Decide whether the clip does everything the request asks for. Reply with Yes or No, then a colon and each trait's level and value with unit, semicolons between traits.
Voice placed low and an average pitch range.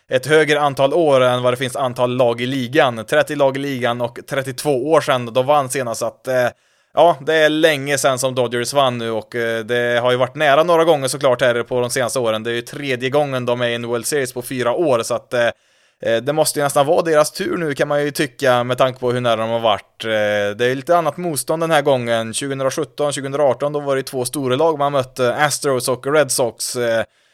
Yes: low, 130 Hz; average, 3.2 semitones